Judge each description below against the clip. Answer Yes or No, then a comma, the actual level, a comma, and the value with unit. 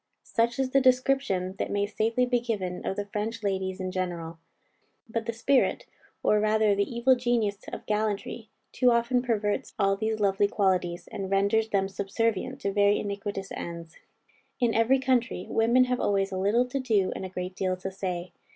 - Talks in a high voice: Yes, high, 210 Hz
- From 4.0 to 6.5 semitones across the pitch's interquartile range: No, average, 3.5 semitones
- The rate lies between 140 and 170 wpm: No, average, 180 wpm